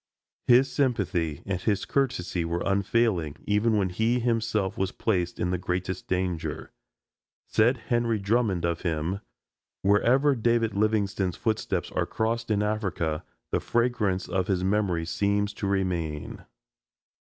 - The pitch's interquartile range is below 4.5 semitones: Yes, average, 4.0 semitones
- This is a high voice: No, low, 100 Hz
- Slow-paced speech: Yes, slow, 130 wpm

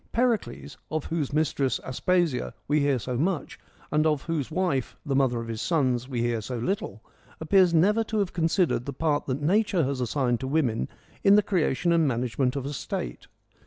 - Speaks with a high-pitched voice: No, medium, 145 Hz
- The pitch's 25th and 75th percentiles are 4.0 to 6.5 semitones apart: Yes, average, 5.0 semitones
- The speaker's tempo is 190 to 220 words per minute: Yes, average, 195 wpm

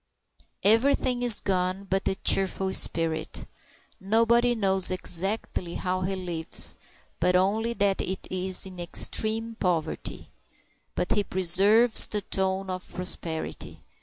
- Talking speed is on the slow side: Yes, slow, 120 wpm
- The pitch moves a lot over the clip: No, average, 3.0 semitones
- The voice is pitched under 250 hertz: Yes, high, 190 Hz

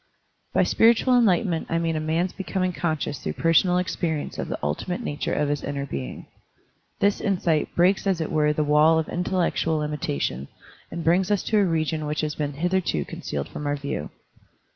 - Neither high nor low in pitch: Yes, medium, 160 Hz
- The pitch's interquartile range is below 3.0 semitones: No, average, 3.4 semitones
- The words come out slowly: No, average, 185 wpm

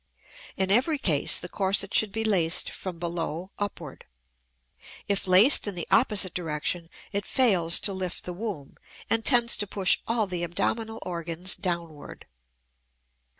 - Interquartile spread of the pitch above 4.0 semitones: No, average, 3.7 semitones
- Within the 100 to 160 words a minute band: Yes, average, 145 wpm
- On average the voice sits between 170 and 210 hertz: Yes, medium, 185 Hz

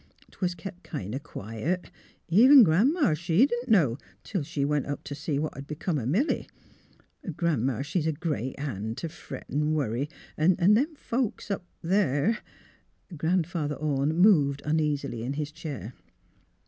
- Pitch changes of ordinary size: Yes, average, 4.6 semitones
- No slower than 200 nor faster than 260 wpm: No, average, 160 wpm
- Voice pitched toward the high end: No, medium, 155 Hz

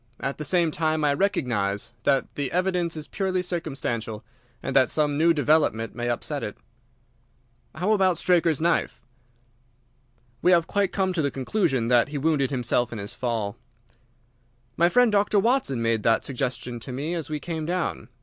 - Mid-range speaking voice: Yes, medium, 150 Hz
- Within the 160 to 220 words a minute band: Yes, average, 170 wpm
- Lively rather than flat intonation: Yes, wide, 6.0 semitones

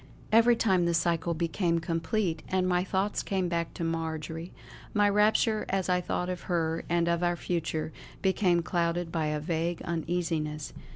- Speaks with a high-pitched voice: No, medium, 170 Hz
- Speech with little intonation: Yes, narrow, 2.0 semitones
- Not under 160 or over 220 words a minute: Yes, average, 165 wpm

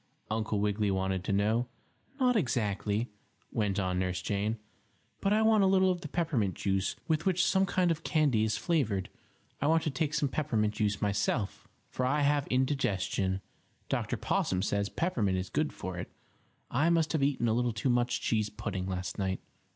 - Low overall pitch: Yes, low, 115 Hz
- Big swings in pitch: Yes, wide, 7.3 semitones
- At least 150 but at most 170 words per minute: No, average, 180 wpm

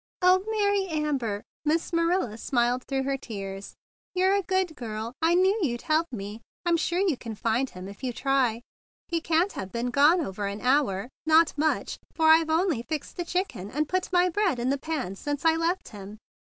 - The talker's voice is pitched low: No, very high, 295 Hz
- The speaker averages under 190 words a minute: No, fast, 205 wpm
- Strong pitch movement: Yes, wide, 6.6 semitones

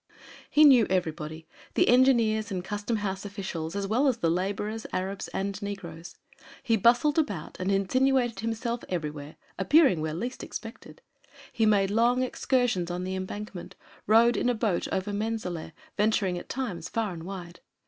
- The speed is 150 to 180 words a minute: Yes, average, 160 wpm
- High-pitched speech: Yes, high, 205 Hz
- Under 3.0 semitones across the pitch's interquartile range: No, average, 4.2 semitones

